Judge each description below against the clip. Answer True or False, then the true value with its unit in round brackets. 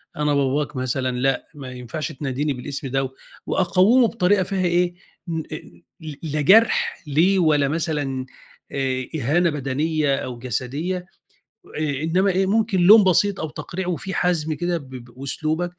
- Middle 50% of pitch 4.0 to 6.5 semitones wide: True (4.9 semitones)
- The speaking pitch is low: False (155 Hz)